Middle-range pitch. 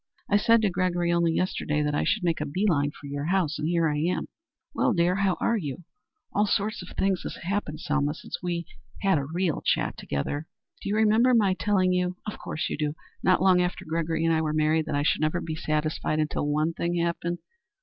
Yes: medium, 170 Hz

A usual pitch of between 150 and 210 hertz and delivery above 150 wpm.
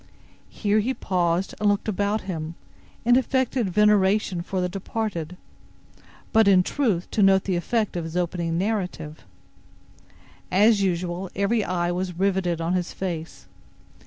No: high, 190 Hz; average, 140 wpm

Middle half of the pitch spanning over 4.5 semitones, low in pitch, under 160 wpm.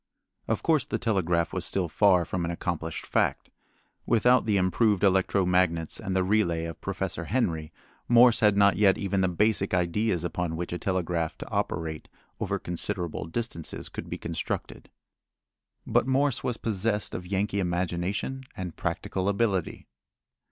No: average, 3.4 semitones; very low, 95 Hz; average, 150 wpm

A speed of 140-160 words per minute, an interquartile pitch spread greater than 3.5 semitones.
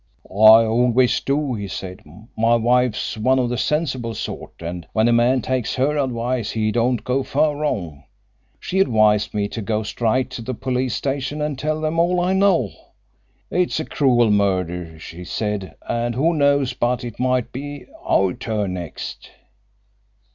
No: average, 170 wpm; average, 4.2 semitones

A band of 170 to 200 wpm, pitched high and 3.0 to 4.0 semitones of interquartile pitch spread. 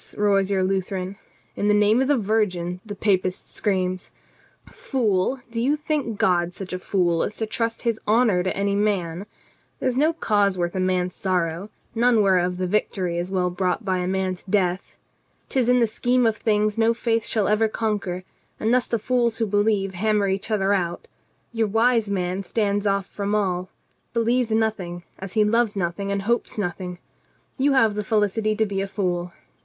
Yes: average, 190 wpm; high, 205 Hz; average, 3.3 semitones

